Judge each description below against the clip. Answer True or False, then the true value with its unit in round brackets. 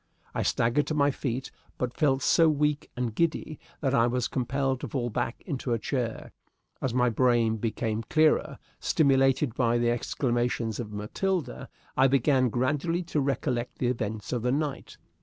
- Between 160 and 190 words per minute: True (165 wpm)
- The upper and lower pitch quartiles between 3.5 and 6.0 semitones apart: False (3.1 semitones)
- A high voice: False (130 Hz)